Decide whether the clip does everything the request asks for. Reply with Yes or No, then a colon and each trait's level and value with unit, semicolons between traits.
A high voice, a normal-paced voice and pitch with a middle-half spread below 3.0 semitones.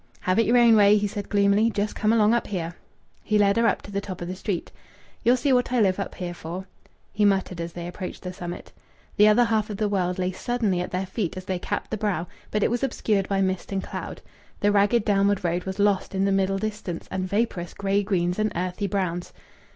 No: high, 200 Hz; fast, 240 wpm; narrow, 2.4 semitones